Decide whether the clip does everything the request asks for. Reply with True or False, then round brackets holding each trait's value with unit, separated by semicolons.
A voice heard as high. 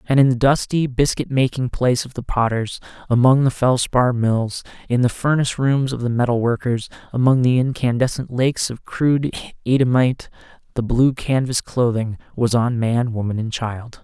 False (125 Hz)